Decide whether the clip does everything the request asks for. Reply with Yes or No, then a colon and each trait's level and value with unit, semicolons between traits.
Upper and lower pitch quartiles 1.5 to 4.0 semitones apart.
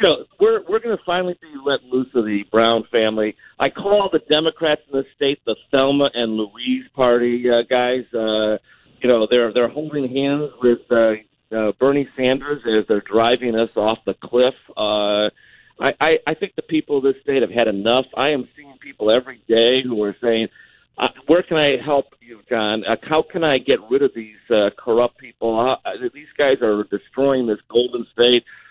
No: average, 4.4 semitones